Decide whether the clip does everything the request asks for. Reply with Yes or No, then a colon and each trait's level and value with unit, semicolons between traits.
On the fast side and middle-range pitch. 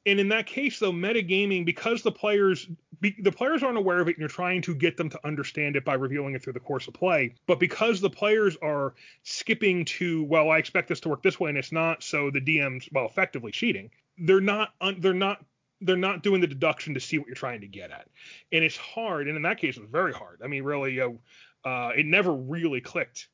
Yes: fast, 245 wpm; medium, 170 Hz